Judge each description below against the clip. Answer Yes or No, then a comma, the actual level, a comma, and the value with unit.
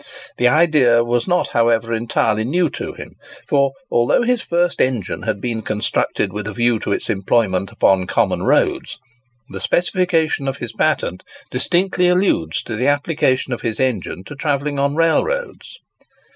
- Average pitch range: No, wide, 6.3 semitones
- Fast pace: No, average, 160 wpm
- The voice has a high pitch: No, low, 130 Hz